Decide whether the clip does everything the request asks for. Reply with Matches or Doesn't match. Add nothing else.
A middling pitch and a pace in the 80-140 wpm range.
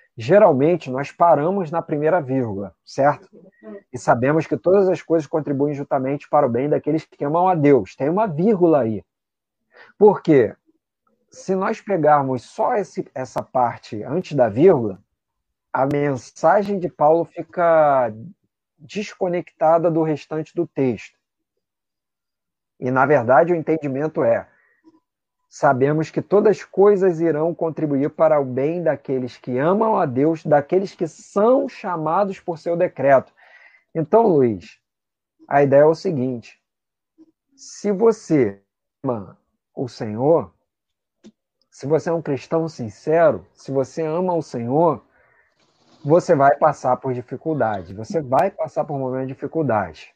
Matches